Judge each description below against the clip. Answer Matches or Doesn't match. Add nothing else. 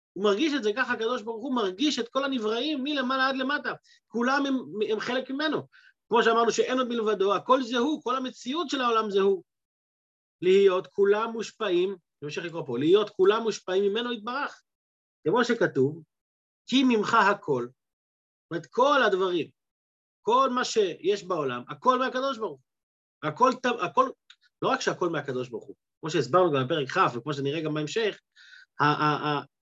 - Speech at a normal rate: Doesn't match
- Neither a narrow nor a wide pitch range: Doesn't match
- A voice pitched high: Matches